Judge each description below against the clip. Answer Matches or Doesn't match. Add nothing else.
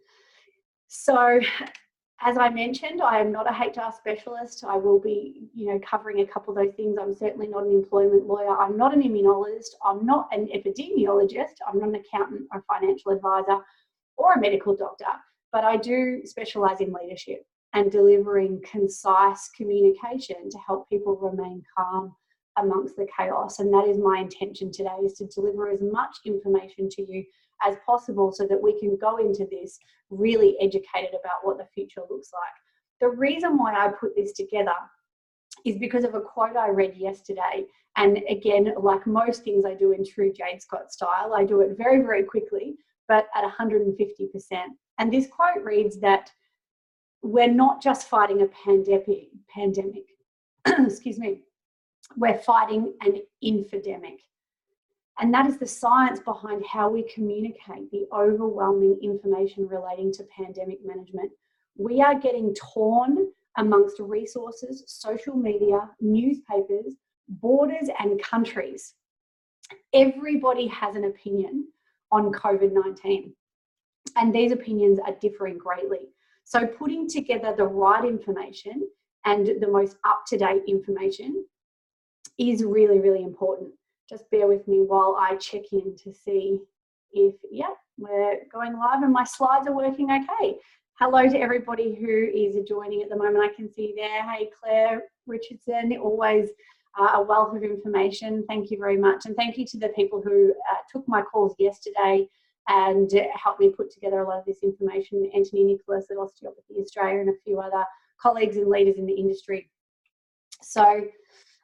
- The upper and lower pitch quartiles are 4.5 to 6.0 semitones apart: Doesn't match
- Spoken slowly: Doesn't match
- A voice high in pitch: Matches